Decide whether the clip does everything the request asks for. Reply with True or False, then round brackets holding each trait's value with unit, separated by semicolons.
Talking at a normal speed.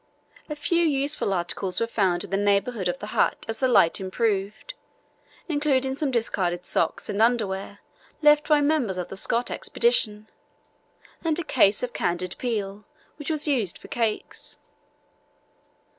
True (150 wpm)